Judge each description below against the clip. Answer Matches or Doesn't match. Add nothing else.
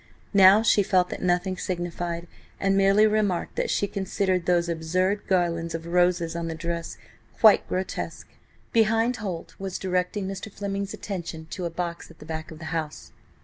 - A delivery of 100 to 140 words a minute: Doesn't match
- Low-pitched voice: Doesn't match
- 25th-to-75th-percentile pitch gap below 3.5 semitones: Matches